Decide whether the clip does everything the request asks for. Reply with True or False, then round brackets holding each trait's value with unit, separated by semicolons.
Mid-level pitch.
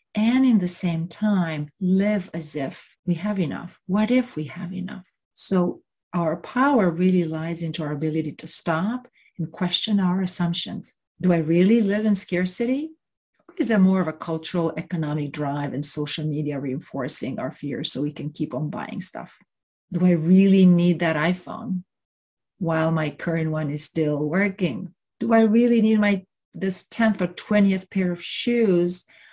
True (180 Hz)